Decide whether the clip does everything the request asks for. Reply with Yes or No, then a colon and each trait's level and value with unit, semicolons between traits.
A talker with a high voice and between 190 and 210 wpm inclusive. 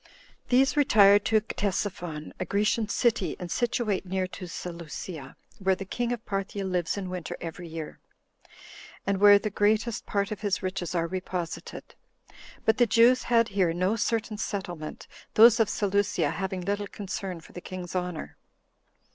No: high, 195 Hz; average, 155 wpm